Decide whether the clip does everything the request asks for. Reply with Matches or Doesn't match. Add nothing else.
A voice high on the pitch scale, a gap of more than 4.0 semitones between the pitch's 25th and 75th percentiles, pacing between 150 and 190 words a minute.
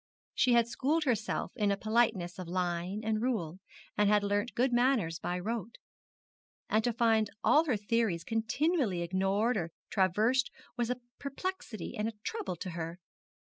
Matches